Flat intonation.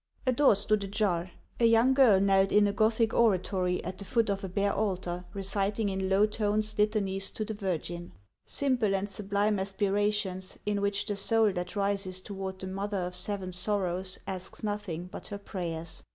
Yes: narrow, 1.9 semitones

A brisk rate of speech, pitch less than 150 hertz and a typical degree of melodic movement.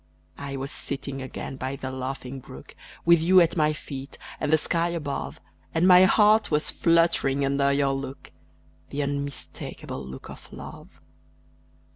No: average, 150 wpm; medium, 140 Hz; average, 3.6 semitones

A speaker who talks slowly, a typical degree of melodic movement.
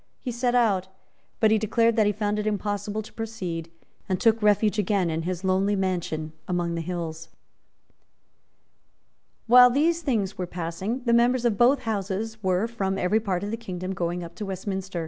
No: average, 175 wpm; average, 3.7 semitones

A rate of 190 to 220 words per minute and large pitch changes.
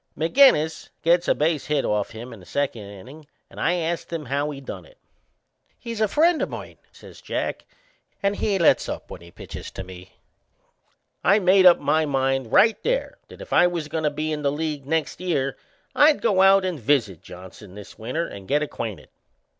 Yes: average, 200 wpm; wide, 6.0 semitones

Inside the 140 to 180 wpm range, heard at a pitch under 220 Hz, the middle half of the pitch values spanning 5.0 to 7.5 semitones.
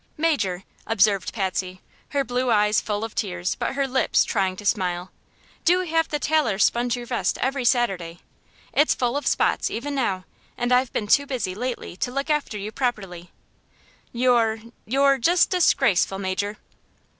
No: average, 160 wpm; high, 235 Hz; wide, 5.6 semitones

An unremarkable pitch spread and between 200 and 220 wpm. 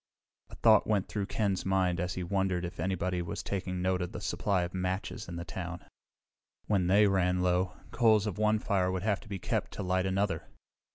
No: narrow, 1.9 semitones; fast, 205 wpm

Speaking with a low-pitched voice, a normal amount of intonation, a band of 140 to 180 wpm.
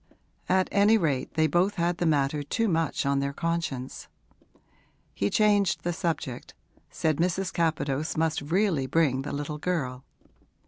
No: medium, 160 Hz; average, 4.0 semitones; average, 145 wpm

